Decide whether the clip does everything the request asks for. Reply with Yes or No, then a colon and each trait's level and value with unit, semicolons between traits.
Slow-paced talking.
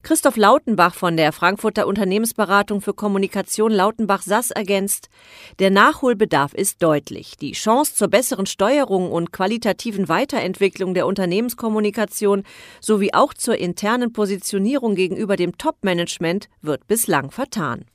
Yes: slow, 120 wpm